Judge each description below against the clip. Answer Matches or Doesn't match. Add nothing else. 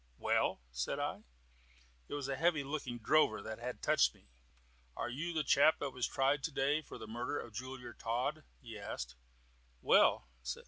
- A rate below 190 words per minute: Matches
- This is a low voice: Matches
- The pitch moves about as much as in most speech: Matches